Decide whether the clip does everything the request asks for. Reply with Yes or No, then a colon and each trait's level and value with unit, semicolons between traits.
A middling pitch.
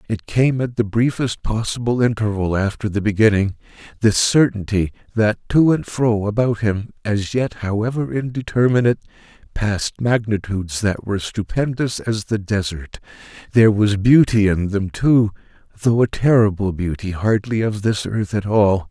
No: low, 110 Hz